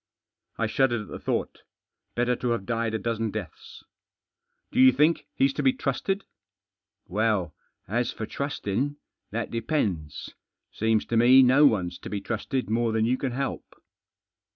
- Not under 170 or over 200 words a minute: Yes, average, 175 wpm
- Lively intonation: No, average, 3.4 semitones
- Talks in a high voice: No, low, 115 Hz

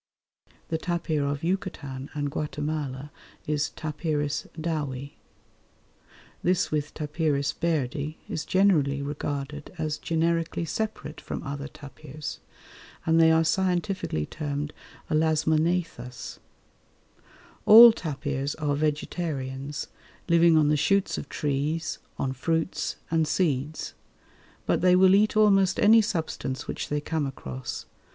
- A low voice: No, medium, 155 Hz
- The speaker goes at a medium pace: No, slow, 115 wpm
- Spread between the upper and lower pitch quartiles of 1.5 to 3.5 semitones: Yes, average, 2.8 semitones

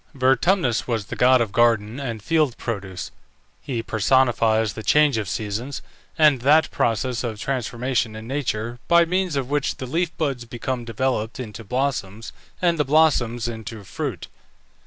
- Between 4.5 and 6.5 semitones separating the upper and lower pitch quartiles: No, average, 3.8 semitones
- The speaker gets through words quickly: No, average, 155 wpm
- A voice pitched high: No, low, 120 Hz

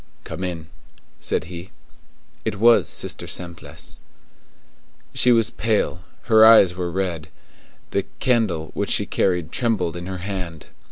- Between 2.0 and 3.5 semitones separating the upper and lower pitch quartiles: No, average, 4.5 semitones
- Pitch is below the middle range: Yes, very low, 90 Hz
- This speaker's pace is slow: Yes, slow, 130 wpm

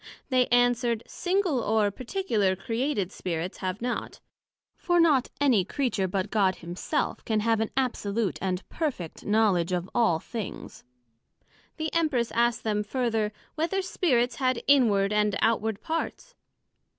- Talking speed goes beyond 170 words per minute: No, slow, 135 wpm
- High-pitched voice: Yes, high, 230 Hz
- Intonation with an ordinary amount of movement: Yes, average, 4.6 semitones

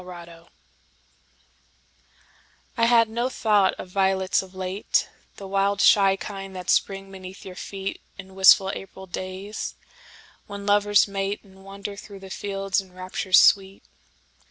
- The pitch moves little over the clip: Yes, narrow, 1.1 semitones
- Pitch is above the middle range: Yes, high, 195 Hz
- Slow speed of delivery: Yes, slow, 125 wpm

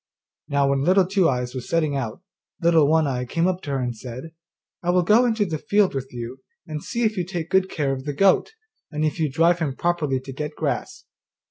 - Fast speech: Yes, fast, 230 wpm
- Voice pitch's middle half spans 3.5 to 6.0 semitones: Yes, average, 4.8 semitones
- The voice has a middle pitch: Yes, medium, 155 Hz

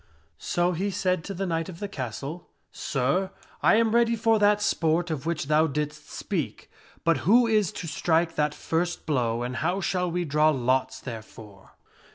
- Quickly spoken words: No, average, 185 wpm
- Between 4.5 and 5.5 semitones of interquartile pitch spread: Yes, average, 4.8 semitones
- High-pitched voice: No, medium, 165 Hz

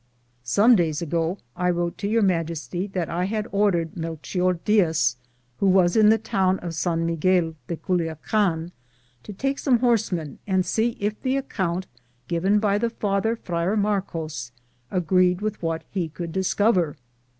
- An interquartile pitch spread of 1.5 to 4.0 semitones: Yes, average, 3.7 semitones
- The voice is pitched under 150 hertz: No, medium, 185 Hz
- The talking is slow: No, average, 155 wpm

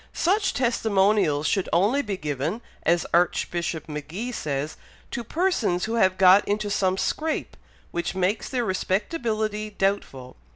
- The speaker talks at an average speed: No, slow, 130 wpm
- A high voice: Yes, high, 195 Hz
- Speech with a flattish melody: No, average, 4.6 semitones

